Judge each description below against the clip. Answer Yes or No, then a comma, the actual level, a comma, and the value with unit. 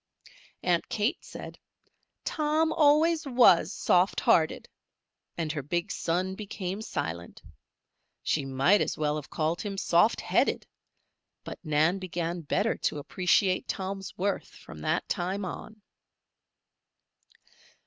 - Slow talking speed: Yes, slow, 120 wpm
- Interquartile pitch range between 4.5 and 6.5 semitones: No, average, 4.0 semitones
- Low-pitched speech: No, medium, 185 Hz